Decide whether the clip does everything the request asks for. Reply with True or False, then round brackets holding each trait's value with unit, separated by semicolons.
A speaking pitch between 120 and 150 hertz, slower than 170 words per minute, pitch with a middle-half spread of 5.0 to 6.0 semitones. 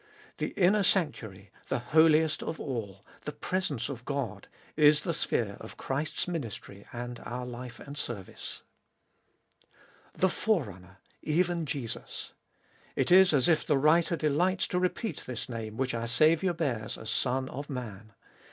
True (140 Hz; 145 wpm; 5.6 semitones)